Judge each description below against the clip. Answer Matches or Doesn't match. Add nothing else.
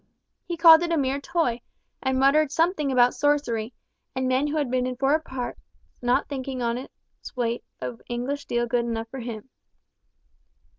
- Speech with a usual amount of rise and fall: Matches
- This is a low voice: Doesn't match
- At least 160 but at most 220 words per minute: Matches